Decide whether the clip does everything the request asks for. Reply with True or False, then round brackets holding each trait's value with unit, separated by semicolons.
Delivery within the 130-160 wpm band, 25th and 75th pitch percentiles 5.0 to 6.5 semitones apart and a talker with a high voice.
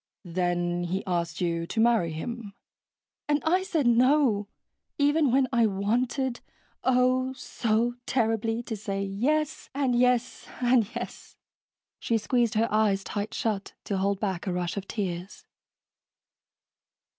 False (135 wpm; 4.4 semitones; 225 Hz)